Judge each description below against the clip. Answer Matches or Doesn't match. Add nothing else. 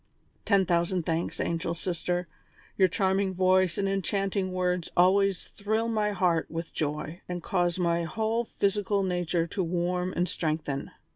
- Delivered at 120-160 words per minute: Matches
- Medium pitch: Matches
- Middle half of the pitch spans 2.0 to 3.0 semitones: Matches